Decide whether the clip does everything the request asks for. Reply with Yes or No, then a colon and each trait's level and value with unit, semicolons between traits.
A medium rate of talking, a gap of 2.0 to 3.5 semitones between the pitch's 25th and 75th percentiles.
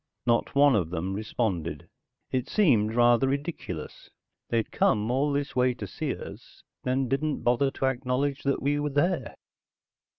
No: average, 155 wpm; average, 4.1 semitones